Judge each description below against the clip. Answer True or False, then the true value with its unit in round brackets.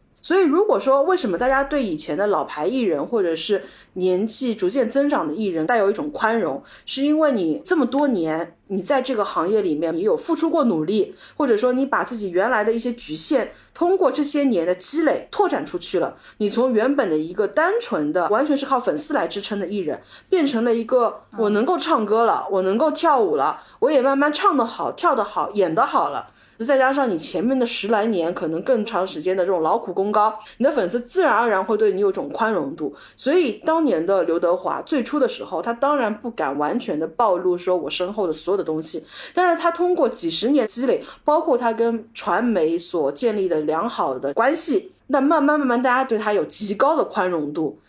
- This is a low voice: False (245 Hz)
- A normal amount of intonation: False (7.2 semitones)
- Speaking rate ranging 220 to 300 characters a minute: False (315 characters per minute)